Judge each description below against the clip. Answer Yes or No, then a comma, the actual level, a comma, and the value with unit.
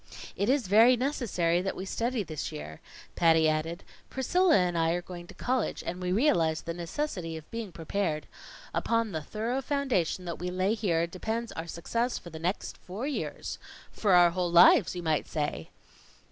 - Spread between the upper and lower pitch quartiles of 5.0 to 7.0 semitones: Yes, wide, 5.5 semitones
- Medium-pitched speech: Yes, medium, 180 Hz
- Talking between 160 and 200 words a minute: Yes, average, 180 wpm